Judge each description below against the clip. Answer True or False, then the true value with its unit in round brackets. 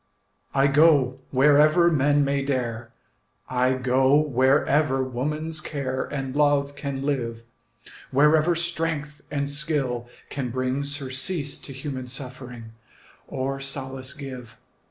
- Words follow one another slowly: True (115 wpm)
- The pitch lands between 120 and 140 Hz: True (135 Hz)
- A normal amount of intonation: False (2.3 semitones)